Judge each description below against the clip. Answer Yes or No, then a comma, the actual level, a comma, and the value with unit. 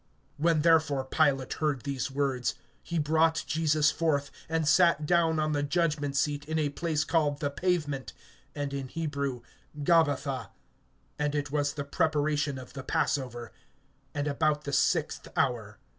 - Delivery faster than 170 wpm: No, average, 150 wpm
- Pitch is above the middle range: No, medium, 145 Hz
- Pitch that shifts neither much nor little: No, narrow, 2.2 semitones